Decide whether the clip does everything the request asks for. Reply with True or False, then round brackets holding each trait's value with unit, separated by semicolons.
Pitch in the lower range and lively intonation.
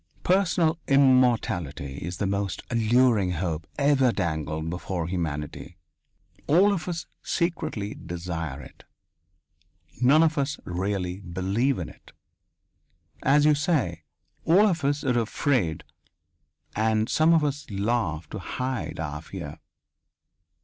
True (110 Hz; 8.5 semitones)